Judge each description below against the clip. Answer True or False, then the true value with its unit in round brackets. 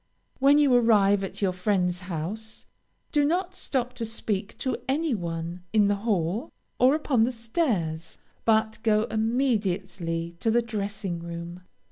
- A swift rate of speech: False (145 wpm)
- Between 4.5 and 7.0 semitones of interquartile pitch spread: True (5.0 semitones)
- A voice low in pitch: False (215 Hz)